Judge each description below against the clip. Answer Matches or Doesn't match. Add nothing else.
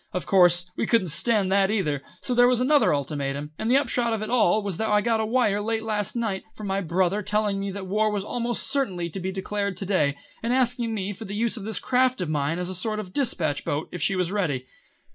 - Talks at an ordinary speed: Doesn't match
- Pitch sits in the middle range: Doesn't match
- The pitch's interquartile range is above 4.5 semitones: Doesn't match